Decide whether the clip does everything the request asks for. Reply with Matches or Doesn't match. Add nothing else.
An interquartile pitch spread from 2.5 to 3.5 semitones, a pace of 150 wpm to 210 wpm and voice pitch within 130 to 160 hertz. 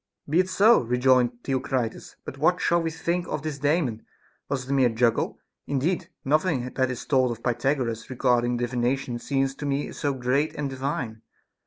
Matches